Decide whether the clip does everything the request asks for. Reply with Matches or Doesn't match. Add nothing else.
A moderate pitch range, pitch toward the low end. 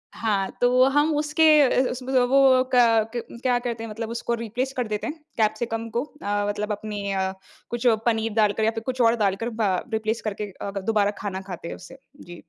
Doesn't match